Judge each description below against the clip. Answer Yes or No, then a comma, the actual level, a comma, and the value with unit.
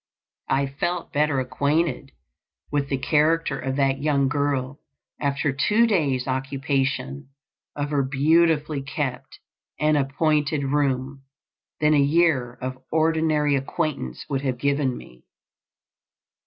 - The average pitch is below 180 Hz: Yes, medium, 140 Hz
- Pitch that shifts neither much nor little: No, narrow, 2.2 semitones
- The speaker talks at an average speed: No, slow, 115 wpm